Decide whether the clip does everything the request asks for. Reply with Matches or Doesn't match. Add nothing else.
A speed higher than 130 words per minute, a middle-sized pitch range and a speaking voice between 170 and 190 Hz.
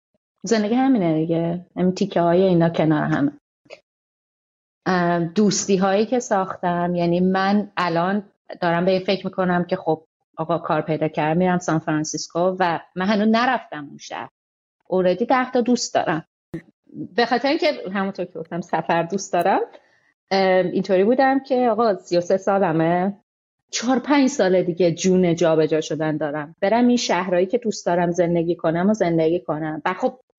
Matches